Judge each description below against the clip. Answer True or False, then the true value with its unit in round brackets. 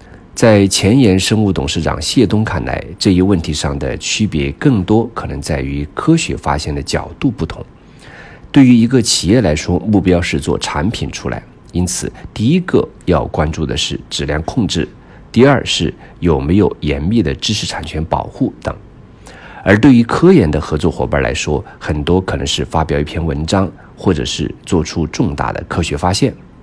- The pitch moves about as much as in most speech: False (5.7 semitones)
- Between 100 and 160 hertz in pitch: False (85 Hz)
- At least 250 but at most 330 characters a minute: True (260 characters per minute)